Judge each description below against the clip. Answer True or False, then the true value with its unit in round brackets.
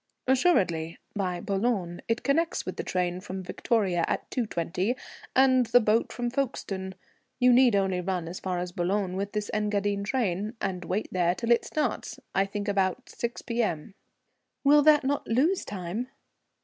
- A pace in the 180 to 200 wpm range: False (160 wpm)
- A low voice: False (205 Hz)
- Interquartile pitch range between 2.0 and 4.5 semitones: False (4.9 semitones)